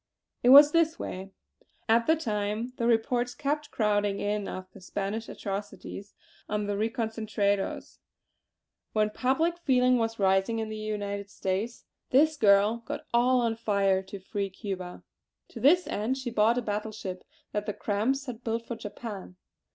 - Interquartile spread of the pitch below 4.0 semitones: Yes, average, 3.3 semitones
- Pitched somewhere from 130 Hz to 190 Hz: No, high, 220 Hz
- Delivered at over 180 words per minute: No, average, 160 wpm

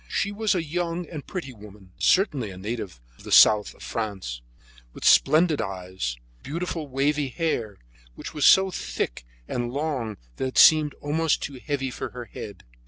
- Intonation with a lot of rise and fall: Yes, wide, 7.2 semitones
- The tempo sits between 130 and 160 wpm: No, average, 170 wpm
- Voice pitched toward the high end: No, low, 135 Hz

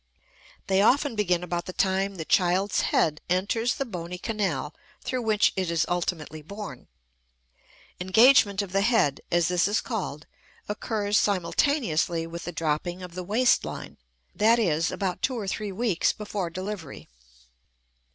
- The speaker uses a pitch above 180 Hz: Yes, high, 190 Hz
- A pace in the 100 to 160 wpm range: Yes, average, 150 wpm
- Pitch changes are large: No, average, 3.6 semitones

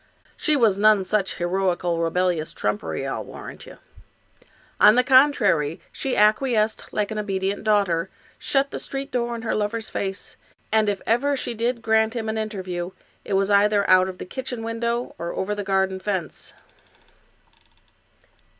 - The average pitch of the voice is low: No, high, 210 Hz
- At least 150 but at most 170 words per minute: Yes, average, 160 wpm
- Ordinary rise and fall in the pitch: Yes, average, 3.4 semitones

